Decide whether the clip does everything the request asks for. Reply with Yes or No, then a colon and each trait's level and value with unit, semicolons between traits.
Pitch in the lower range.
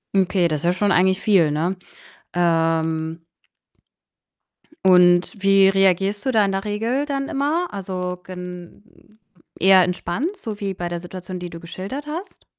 No: medium, 185 Hz